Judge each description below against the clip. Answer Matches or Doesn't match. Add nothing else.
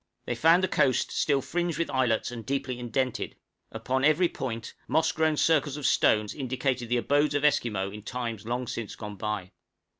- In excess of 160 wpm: Matches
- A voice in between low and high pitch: Doesn't match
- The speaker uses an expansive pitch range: Doesn't match